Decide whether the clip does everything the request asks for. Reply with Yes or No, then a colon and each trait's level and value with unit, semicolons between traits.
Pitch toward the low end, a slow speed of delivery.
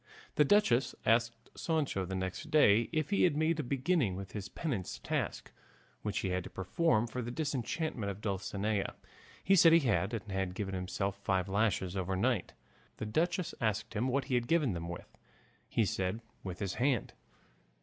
No: low, 110 Hz; average, 180 wpm